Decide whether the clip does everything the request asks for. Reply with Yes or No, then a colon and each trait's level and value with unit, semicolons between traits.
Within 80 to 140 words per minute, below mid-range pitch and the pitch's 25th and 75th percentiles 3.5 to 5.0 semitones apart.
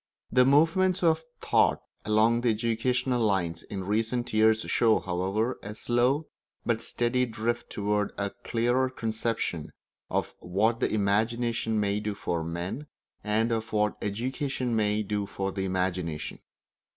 No: slow, 135 wpm; low, 110 Hz; average, 3.0 semitones